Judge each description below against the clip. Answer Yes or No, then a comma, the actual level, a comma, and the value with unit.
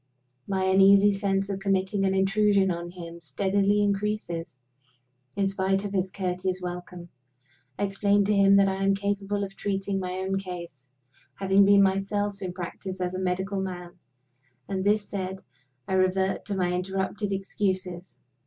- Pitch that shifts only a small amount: Yes, narrow, 1.3 semitones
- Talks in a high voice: Yes, high, 195 Hz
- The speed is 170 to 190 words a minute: No, average, 155 wpm